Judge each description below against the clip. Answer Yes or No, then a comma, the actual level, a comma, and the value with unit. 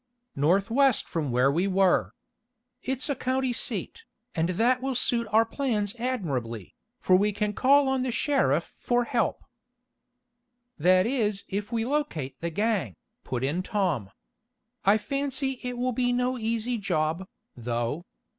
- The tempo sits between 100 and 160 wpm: Yes, average, 145 wpm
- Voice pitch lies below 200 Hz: No, high, 215 Hz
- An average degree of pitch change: No, wide, 6.9 semitones